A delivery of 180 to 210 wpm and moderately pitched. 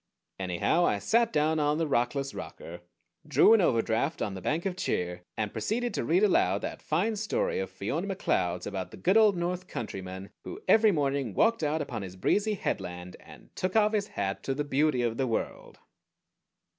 Yes: average, 190 wpm; medium, 150 Hz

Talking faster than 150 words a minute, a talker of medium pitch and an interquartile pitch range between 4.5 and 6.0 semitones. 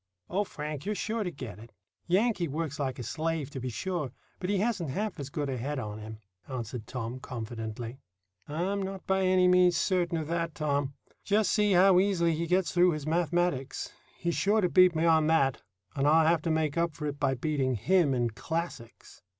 Yes: fast, 205 wpm; medium, 160 Hz; average, 5.1 semitones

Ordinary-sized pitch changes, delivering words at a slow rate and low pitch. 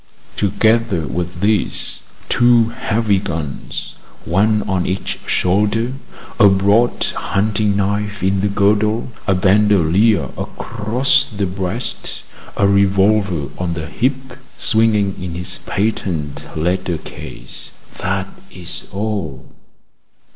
Yes: average, 3.0 semitones; slow, 105 wpm; low, 100 Hz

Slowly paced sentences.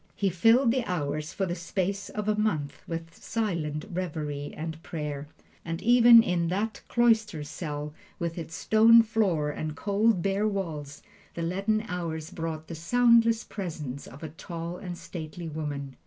No: average, 155 wpm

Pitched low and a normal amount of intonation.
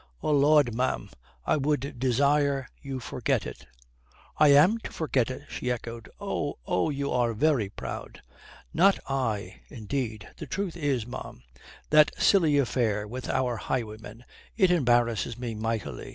Yes: low, 130 Hz; average, 4.1 semitones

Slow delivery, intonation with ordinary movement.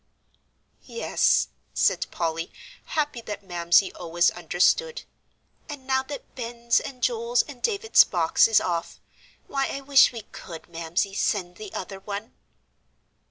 No: slow, 130 wpm; wide, 7.0 semitones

